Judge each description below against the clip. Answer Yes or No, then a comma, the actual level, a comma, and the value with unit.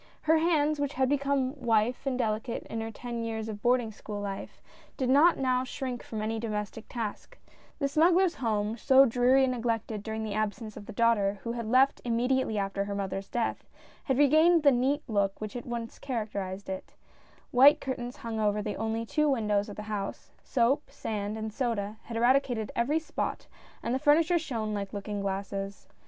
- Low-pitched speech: No, high, 230 Hz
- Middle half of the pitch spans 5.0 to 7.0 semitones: No, average, 3.9 semitones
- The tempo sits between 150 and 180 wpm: No, average, 190 wpm